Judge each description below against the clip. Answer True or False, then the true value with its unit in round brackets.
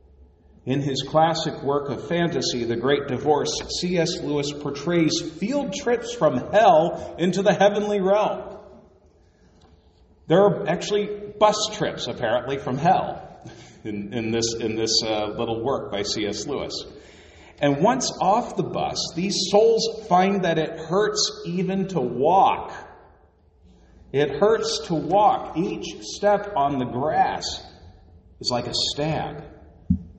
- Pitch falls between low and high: True (150 Hz)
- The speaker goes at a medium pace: False (125 wpm)